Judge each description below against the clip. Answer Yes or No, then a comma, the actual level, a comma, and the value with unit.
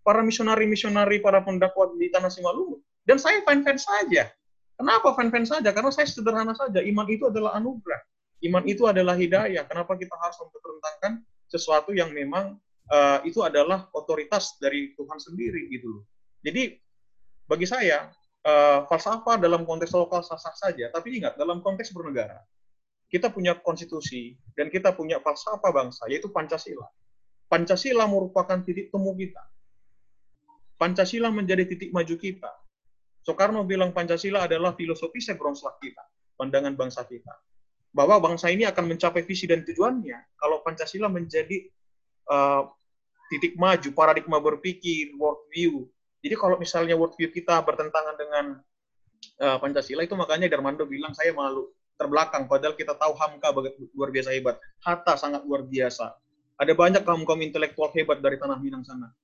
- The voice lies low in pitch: No, medium, 170 Hz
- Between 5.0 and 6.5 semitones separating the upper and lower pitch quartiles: Yes, wide, 5.4 semitones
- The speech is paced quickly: Yes, fast, 145 wpm